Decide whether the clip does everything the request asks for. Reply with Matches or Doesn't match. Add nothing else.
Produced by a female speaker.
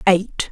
Matches